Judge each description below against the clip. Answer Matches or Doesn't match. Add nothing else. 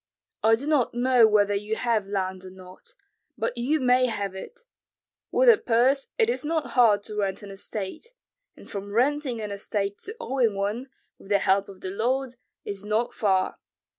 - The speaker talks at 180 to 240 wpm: Matches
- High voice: Matches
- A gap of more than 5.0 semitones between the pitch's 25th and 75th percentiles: Doesn't match